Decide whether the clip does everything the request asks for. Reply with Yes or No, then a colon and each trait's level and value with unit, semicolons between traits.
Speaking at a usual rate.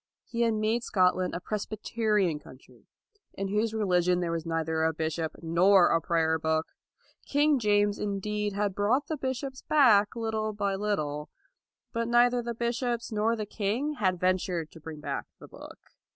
Yes: average, 165 wpm